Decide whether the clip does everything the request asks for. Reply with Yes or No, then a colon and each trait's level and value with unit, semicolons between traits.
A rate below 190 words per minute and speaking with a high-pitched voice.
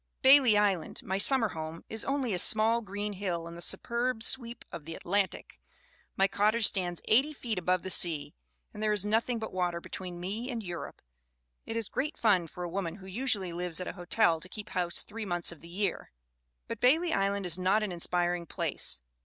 No: fast, 205 wpm; high, 195 Hz